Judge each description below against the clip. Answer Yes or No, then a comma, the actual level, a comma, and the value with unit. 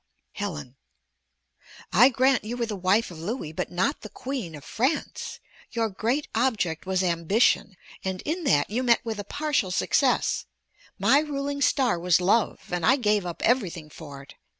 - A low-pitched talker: No, high, 210 Hz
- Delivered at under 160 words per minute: No, average, 170 wpm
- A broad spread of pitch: Yes, wide, 6.3 semitones